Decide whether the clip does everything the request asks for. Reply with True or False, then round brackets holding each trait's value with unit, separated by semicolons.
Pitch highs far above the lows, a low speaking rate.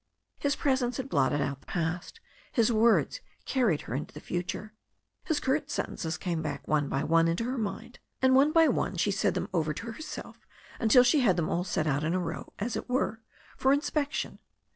False (8.1 semitones; 205 wpm)